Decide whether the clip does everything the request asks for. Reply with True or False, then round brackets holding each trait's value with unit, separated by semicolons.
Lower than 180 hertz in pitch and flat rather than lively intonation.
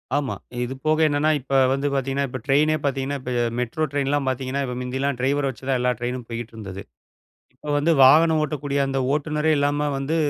True (140 Hz; 2.2 semitones)